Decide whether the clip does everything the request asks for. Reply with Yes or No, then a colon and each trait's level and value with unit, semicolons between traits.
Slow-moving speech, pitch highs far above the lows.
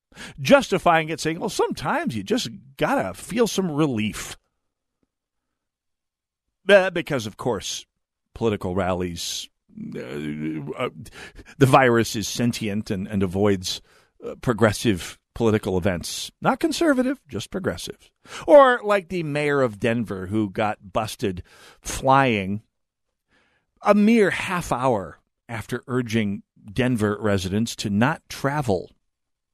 Yes: slow, 110 wpm; wide, 8.0 semitones